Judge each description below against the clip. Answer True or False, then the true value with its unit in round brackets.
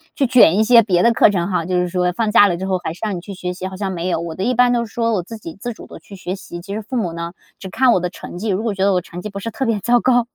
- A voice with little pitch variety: False (4.2 semitones)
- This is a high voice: True (195 Hz)